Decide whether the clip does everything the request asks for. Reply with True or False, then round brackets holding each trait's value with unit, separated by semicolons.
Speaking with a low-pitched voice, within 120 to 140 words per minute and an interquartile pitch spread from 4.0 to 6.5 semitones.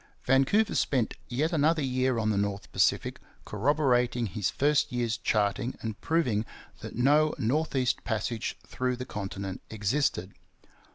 True (125 Hz; 135 wpm; 4.8 semitones)